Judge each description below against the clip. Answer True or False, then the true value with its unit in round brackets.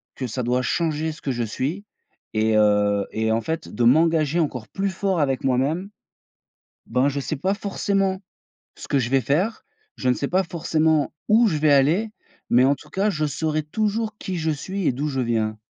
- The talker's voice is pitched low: False (150 Hz)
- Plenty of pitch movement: True (6.3 semitones)